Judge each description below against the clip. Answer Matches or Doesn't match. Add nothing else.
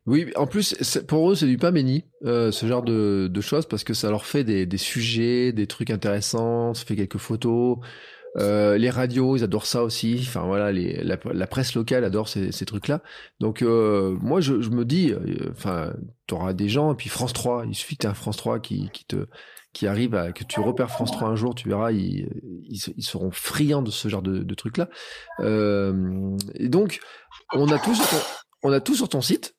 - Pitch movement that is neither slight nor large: Matches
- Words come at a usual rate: Doesn't match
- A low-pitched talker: Matches